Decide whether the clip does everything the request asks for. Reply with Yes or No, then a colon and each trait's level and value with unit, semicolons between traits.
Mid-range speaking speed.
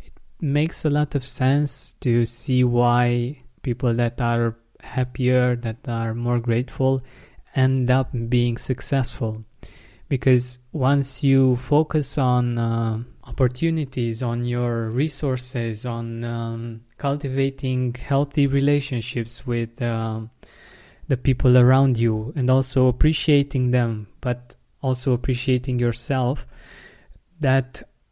No: slow, 105 wpm